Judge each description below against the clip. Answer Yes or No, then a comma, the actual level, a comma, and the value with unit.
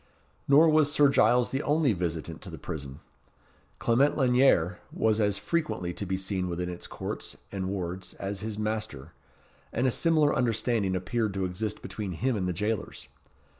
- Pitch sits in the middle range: No, low, 105 Hz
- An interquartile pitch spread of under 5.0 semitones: No, wide, 5.4 semitones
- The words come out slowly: No, average, 170 wpm